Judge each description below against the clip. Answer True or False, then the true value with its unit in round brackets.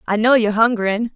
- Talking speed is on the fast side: True (210 wpm)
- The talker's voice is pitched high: True (220 Hz)